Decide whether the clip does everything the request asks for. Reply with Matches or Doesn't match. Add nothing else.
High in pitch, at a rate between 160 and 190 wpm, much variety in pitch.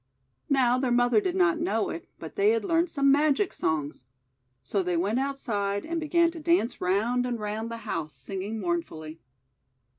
Matches